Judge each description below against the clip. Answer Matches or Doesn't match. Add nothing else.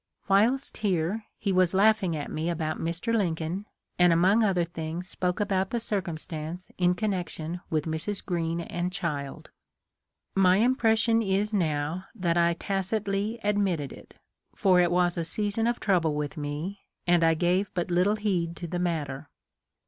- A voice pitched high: Doesn't match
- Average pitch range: Matches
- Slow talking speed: Doesn't match